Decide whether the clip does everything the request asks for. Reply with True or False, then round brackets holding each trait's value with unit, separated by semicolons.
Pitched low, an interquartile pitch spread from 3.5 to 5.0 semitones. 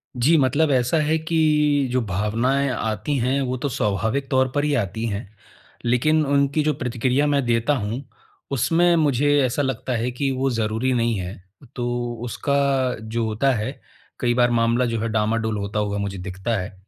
True (125 Hz; 3.8 semitones)